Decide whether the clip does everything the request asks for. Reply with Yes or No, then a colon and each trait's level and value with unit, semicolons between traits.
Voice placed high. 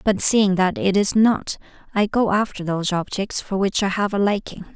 Yes: high, 195 Hz